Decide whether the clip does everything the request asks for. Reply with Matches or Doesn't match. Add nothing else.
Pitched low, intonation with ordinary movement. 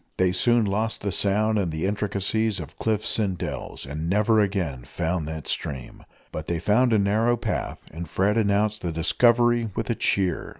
Matches